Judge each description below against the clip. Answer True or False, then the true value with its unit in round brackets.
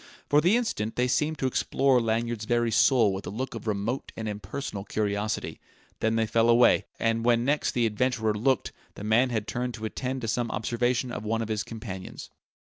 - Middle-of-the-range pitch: False (115 Hz)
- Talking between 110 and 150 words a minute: False (200 wpm)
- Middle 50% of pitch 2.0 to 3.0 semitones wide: True (2.5 semitones)